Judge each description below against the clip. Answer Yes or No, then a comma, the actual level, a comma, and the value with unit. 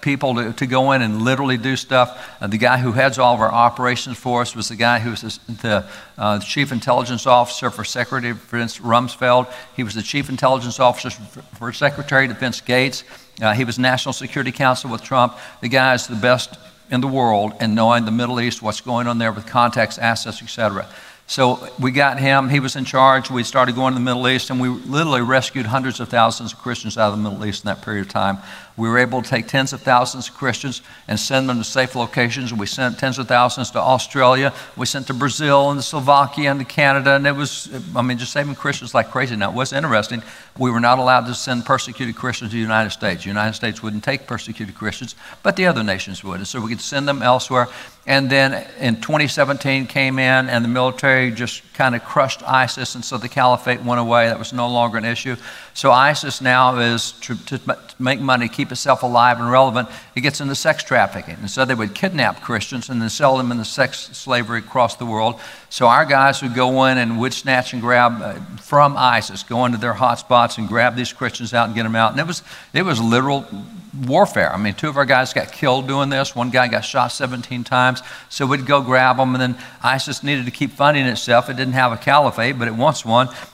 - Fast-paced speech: Yes, fast, 230 wpm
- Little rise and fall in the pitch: Yes, narrow, 2.1 semitones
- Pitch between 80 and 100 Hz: No, low, 125 Hz